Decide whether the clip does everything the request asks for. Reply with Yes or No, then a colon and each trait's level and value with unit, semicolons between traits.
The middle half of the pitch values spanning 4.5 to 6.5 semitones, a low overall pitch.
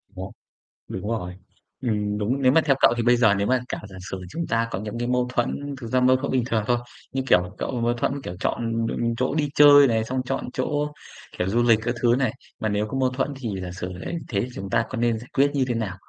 No: average, 3.4 semitones; low, 120 Hz